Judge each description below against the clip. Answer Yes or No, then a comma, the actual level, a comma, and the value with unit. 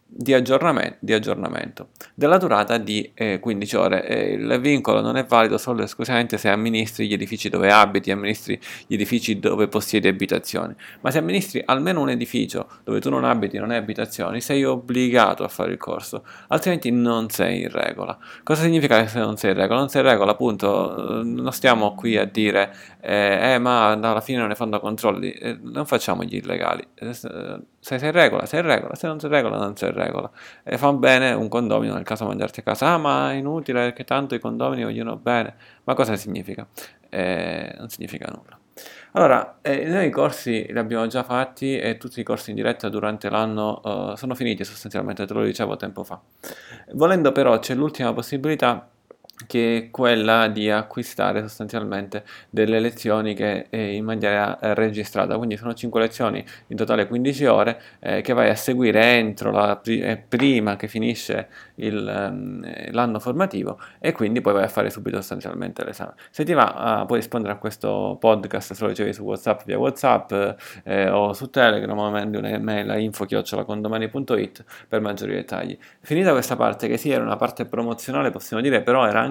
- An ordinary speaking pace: No, fast, 185 wpm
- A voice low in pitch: Yes, low, 115 Hz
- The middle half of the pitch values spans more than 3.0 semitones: No, narrow, 2.6 semitones